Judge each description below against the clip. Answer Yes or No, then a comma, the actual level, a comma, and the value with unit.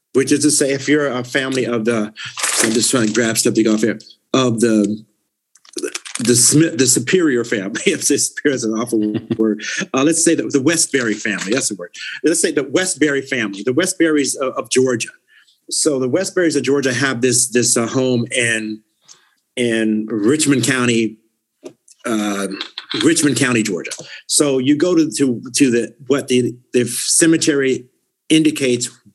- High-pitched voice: No, low, 125 Hz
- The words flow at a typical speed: Yes, average, 170 wpm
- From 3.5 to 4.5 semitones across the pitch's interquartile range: Yes, average, 4.0 semitones